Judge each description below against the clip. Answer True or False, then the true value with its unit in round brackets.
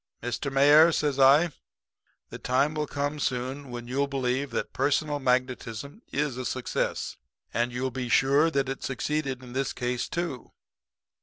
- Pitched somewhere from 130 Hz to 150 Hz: True (135 Hz)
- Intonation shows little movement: True (2.3 semitones)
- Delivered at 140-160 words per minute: True (155 wpm)